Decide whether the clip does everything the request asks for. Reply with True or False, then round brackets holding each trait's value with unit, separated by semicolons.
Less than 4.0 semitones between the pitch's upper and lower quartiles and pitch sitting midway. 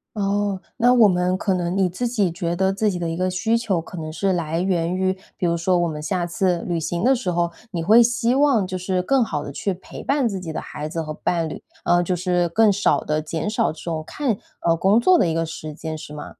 True (3.4 semitones; 180 Hz)